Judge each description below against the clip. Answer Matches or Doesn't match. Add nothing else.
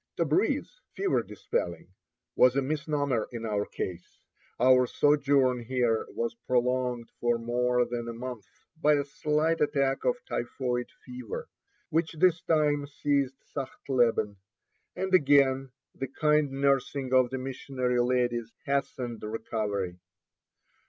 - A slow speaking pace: Matches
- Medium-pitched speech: Doesn't match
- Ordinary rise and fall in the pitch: Matches